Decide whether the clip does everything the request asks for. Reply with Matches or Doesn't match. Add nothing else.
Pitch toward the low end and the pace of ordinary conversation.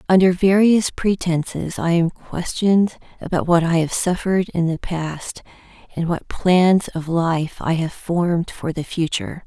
Doesn't match